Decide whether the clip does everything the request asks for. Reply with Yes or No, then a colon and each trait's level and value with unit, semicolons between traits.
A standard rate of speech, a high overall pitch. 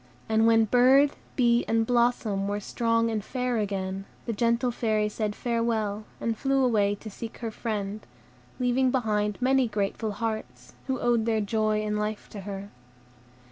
Yes: average, 160 wpm; high, 225 Hz